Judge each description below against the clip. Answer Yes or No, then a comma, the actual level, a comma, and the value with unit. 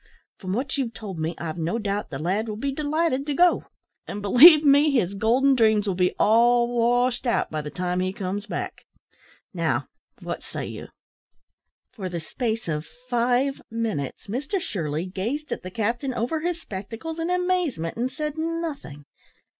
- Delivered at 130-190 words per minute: Yes, average, 170 wpm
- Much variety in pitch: Yes, wide, 6.8 semitones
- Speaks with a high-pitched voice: Yes, high, 230 Hz